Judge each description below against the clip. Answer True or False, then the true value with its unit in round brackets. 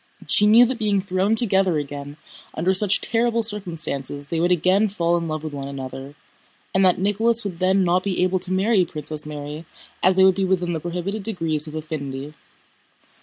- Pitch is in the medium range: True (180 Hz)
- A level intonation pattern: False (4.3 semitones)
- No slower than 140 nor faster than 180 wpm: False (190 wpm)